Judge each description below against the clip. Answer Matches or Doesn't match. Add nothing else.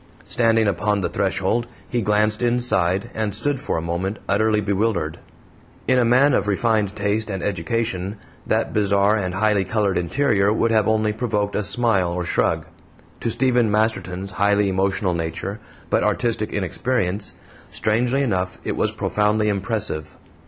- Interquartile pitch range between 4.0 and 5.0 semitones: Doesn't match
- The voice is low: Matches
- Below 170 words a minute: Matches